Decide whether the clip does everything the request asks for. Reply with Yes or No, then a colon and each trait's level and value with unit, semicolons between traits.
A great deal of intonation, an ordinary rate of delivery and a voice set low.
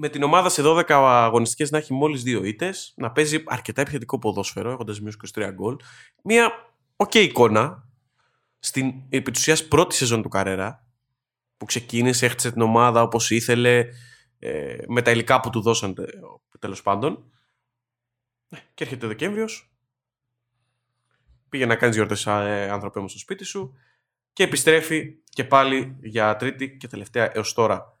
No: average, 3.7 semitones; average, 150 wpm; low, 125 Hz